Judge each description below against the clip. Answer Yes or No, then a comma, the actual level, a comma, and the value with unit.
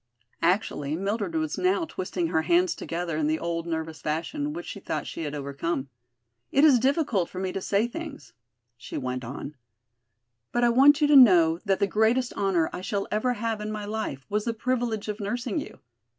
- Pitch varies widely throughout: Yes, wide, 6.6 semitones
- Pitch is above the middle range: Yes, high, 200 Hz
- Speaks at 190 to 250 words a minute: Yes, average, 195 wpm